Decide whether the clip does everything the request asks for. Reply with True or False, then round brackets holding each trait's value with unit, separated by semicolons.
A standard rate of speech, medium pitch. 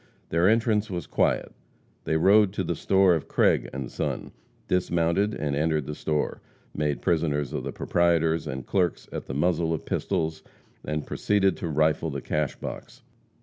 False (165 wpm; 80 Hz)